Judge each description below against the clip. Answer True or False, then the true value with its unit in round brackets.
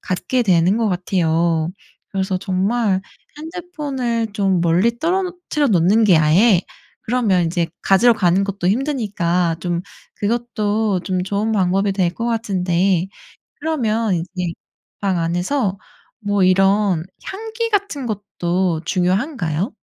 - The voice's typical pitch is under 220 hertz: True (195 Hz)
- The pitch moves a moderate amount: True (4.7 semitones)